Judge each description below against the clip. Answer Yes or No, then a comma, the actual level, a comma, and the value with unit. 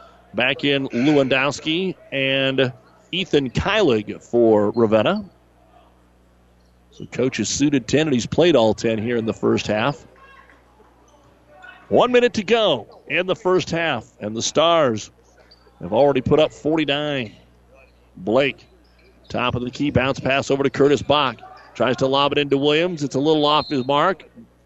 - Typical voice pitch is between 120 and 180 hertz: Yes, low, 135 Hz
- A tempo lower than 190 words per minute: Yes, average, 150 wpm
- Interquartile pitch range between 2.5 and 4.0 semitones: No, average, 5.0 semitones